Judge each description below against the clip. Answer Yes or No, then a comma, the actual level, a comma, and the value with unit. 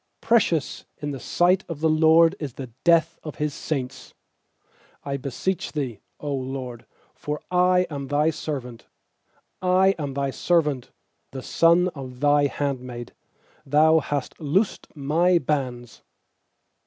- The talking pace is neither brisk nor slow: No, slow, 130 wpm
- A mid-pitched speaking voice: Yes, medium, 145 Hz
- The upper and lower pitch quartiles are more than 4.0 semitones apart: No, average, 3.6 semitones